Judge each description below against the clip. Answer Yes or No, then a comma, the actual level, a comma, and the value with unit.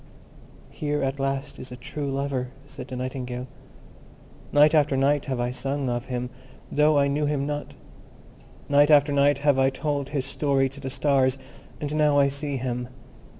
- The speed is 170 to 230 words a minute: Yes, average, 175 wpm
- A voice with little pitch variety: Yes, narrow, 1.8 semitones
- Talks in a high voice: No, medium, 140 Hz